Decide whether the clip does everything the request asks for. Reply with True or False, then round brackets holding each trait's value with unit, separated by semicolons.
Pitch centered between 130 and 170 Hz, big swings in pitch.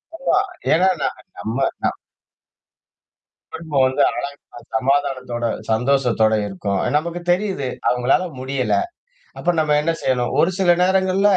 True (140 Hz; 5.9 semitones)